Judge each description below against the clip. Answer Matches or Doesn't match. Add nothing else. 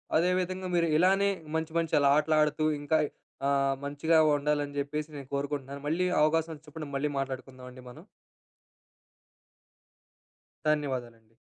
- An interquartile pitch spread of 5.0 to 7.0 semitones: Doesn't match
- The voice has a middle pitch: Matches